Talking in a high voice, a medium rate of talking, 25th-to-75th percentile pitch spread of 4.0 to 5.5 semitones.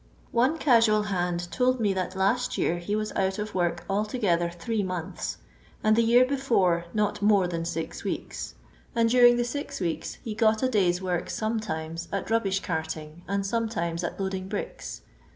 Yes: high, 200 Hz; average, 170 wpm; average, 4.6 semitones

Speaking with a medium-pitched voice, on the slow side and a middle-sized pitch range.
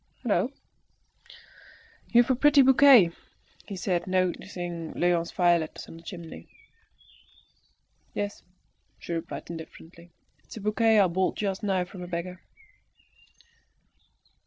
Yes: medium, 180 Hz; slow, 110 wpm; average, 3.3 semitones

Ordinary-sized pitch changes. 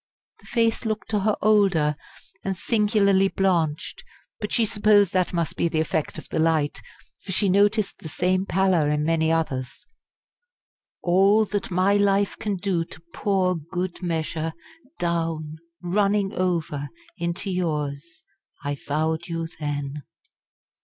Yes: average, 3.9 semitones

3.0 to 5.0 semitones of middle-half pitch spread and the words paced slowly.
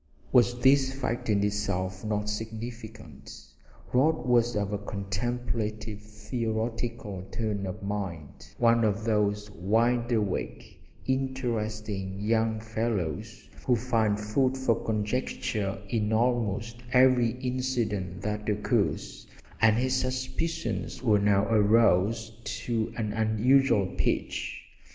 No: narrow, 2.6 semitones; slow, 110 wpm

